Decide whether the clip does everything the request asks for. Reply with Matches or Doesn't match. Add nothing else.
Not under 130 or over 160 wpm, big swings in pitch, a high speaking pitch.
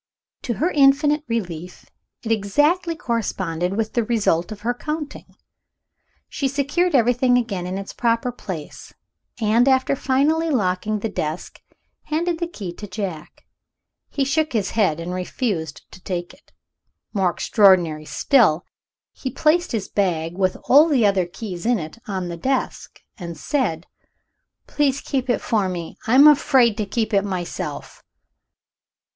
Matches